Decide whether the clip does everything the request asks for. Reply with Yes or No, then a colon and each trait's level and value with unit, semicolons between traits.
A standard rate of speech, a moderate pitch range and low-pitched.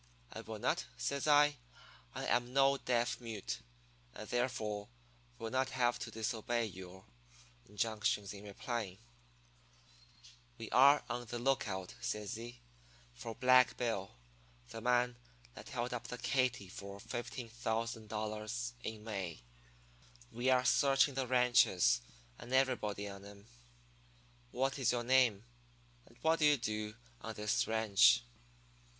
No: slow, 130 wpm; average, 3.3 semitones; low, 115 Hz